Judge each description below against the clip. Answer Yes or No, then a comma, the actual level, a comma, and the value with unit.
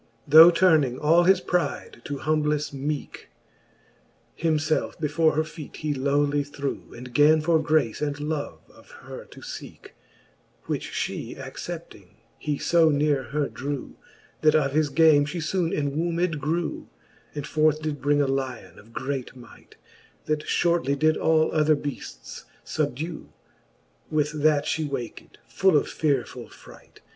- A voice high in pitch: No, medium, 150 Hz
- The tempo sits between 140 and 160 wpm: Yes, average, 150 wpm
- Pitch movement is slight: Yes, narrow, 1.9 semitones